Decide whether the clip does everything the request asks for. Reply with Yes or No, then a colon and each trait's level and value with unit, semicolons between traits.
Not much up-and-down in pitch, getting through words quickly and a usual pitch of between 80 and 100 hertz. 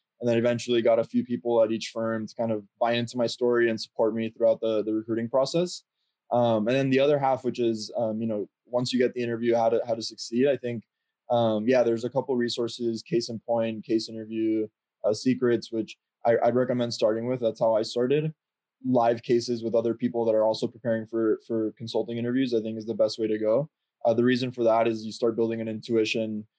No: narrow, 1.4 semitones; fast, 230 wpm; low, 115 Hz